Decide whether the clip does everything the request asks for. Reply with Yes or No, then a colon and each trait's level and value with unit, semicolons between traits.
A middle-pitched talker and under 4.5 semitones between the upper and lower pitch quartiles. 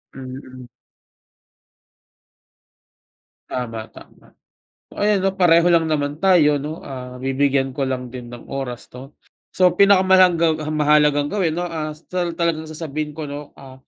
Yes: medium, 150 Hz; average, 3.9 semitones